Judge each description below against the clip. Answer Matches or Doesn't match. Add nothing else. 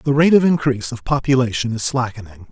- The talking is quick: Doesn't match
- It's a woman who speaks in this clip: Doesn't match